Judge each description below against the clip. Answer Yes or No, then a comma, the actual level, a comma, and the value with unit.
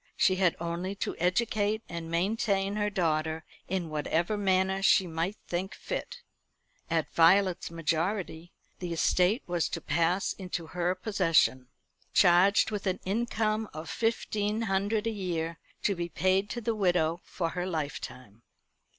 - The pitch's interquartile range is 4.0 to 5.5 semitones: No, average, 3.4 semitones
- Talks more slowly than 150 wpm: Yes, average, 140 wpm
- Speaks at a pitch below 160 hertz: No, medium, 185 Hz